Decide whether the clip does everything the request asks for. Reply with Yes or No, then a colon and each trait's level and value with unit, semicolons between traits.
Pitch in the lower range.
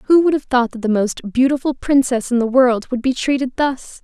No: very high, 255 Hz